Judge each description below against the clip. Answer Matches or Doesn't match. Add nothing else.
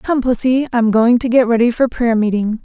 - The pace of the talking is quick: Matches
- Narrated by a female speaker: Matches